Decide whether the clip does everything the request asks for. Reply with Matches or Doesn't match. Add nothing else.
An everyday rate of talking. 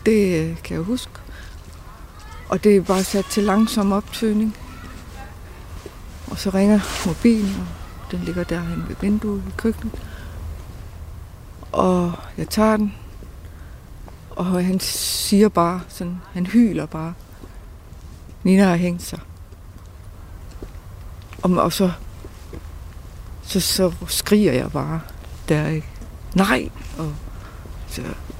Doesn't match